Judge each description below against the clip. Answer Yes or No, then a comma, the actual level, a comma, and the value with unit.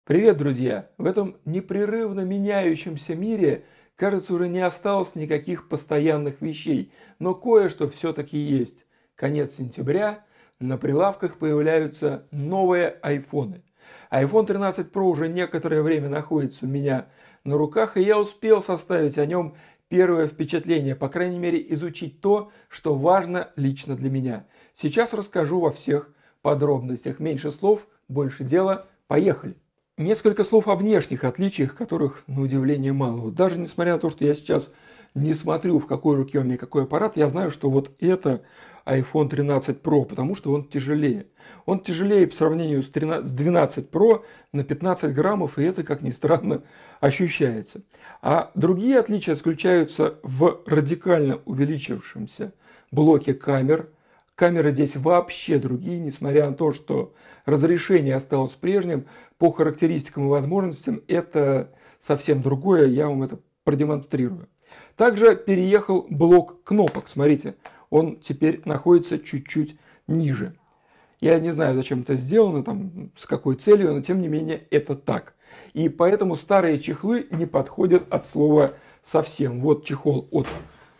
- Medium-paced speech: Yes, average, 140 wpm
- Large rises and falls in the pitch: No, average, 4.2 semitones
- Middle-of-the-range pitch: Yes, medium, 160 Hz